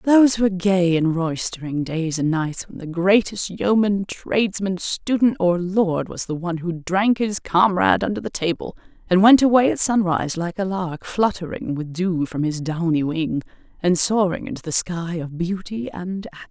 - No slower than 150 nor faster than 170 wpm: No, average, 180 wpm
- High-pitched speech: No, medium, 180 Hz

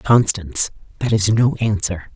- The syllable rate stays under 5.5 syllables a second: Yes, 4.4 syllables/s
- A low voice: Yes, low, 105 Hz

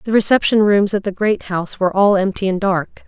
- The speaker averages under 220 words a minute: No, fast, 235 wpm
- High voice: Yes, high, 200 Hz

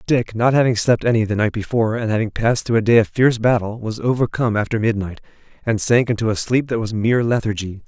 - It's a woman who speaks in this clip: No, male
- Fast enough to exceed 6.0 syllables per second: Yes, 6.5 syllables/s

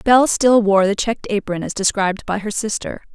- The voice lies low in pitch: No, high, 210 Hz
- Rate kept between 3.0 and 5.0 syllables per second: No, 5.5 syllables/s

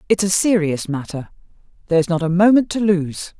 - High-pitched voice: No, medium, 180 Hz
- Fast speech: No, average, 175 wpm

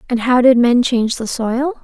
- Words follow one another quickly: Yes, fast, 230 wpm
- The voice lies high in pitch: Yes, high, 245 Hz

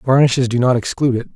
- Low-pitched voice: Yes, low, 125 Hz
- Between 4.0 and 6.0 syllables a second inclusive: No, 7.1 syllables/s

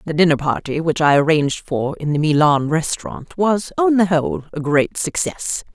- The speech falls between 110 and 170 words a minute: No, average, 190 wpm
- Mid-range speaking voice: Yes, medium, 160 Hz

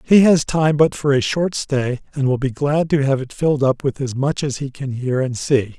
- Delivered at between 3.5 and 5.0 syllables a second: Yes, 4.9 syllables/s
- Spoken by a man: Yes, male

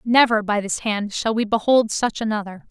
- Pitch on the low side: No, high, 215 Hz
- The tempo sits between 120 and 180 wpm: No, average, 200 wpm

